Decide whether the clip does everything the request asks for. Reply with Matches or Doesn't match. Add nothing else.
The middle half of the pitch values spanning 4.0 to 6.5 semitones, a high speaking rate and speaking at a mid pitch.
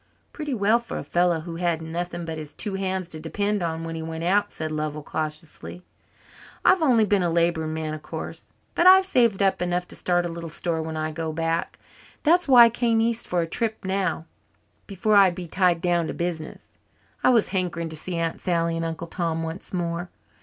Doesn't match